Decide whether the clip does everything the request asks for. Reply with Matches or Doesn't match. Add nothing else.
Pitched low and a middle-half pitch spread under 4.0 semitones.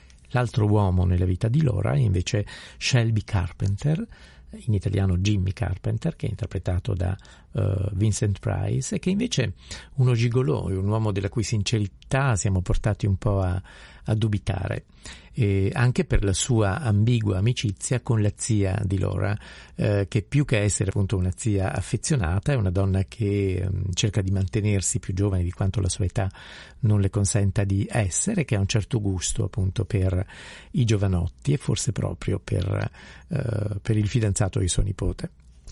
Matches